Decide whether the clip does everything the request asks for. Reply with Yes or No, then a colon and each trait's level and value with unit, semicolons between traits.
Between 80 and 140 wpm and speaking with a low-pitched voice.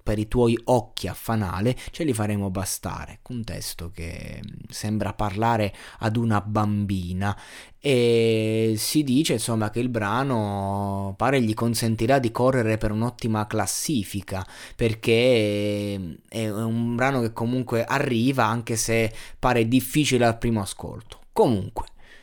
Yes: average, 130 wpm; low, 110 Hz